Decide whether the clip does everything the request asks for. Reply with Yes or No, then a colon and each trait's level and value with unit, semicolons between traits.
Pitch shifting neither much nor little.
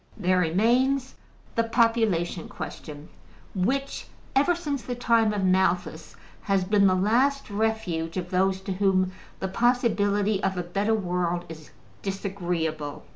Yes: average, 4.2 semitones